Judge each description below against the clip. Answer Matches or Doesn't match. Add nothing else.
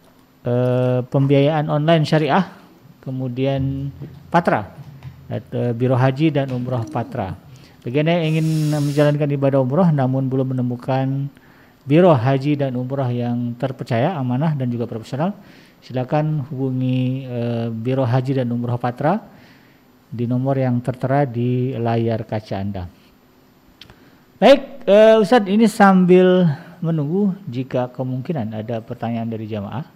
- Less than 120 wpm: Matches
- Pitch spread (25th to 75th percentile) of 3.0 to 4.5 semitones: Matches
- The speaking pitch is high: Doesn't match